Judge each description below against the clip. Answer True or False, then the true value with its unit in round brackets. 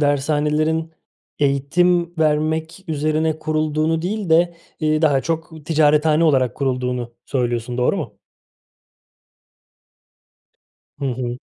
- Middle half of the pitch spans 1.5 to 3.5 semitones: True (2.6 semitones)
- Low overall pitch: False (155 Hz)